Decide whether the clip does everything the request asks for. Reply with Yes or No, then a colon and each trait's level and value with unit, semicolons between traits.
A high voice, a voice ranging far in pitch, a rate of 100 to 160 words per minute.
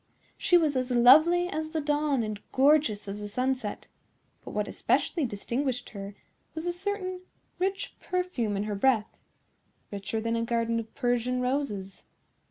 Yes: very high, 250 Hz; wide, 6.0 semitones; average, 150 wpm